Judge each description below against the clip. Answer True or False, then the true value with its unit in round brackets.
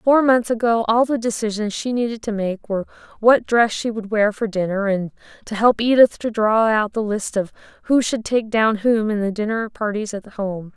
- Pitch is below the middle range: False (220 Hz)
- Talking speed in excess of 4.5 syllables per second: True (5.0 syllables/s)